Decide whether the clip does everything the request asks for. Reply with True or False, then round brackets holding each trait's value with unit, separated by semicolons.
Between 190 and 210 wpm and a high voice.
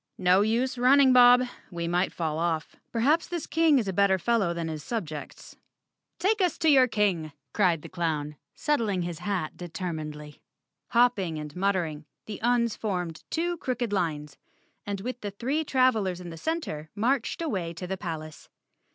False (170 wpm; 195 Hz)